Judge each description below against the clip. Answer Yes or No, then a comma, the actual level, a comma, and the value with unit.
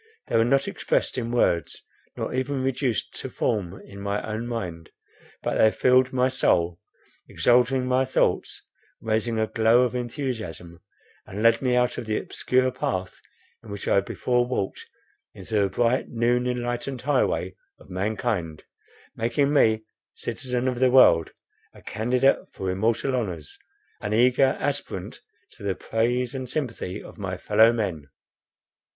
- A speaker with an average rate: Yes, average, 150 wpm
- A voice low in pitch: Yes, low, 115 Hz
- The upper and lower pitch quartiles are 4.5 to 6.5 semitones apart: No, average, 3.8 semitones